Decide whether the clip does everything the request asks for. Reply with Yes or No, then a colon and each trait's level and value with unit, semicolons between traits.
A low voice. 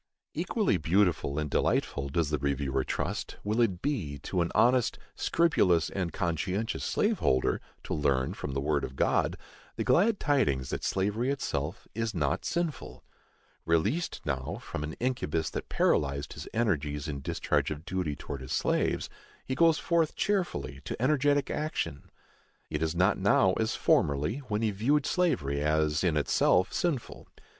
Yes: very low, 90 Hz